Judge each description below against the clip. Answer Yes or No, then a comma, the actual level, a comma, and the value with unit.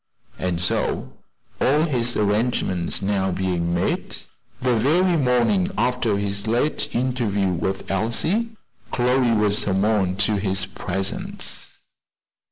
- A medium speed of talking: No, slow, 110 wpm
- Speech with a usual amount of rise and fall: Yes, average, 4.6 semitones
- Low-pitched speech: Yes, low, 105 Hz